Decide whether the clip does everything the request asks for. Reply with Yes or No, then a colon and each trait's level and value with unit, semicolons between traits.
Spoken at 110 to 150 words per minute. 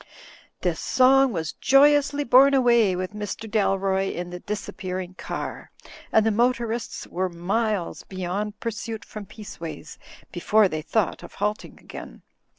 Yes: average, 140 wpm